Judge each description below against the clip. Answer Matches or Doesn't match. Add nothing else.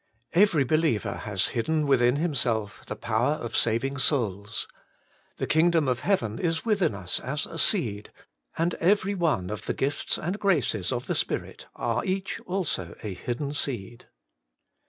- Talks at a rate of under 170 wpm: Matches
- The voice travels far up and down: Matches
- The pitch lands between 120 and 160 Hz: Matches